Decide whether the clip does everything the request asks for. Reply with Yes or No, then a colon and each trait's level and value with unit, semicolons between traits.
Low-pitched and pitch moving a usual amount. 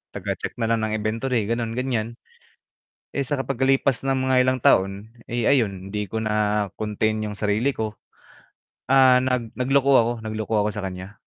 Yes: low, 115 Hz; average, 3.2 semitones